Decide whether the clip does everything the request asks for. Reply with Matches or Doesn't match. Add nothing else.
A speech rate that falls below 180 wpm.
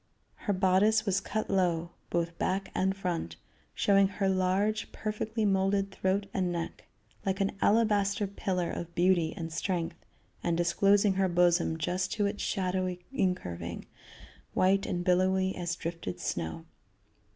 Matches